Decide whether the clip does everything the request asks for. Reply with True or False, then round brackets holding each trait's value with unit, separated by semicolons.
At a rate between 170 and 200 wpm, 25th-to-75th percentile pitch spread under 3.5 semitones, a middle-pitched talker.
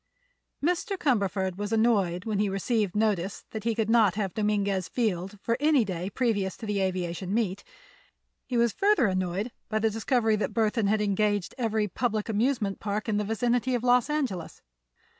False (175 wpm; 3.0 semitones; 215 Hz)